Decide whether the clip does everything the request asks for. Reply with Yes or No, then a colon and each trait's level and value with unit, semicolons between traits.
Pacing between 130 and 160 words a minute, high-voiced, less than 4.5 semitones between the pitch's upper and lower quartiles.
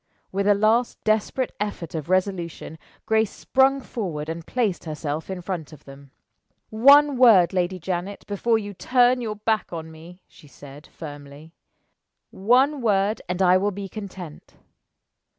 No: average, 150 wpm; high, 195 Hz; average, 5.1 semitones